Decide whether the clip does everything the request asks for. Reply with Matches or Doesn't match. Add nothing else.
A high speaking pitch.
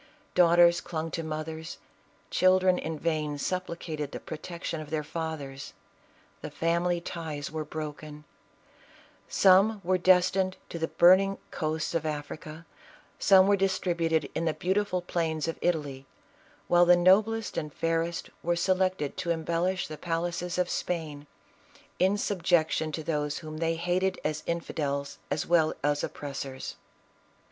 Doesn't match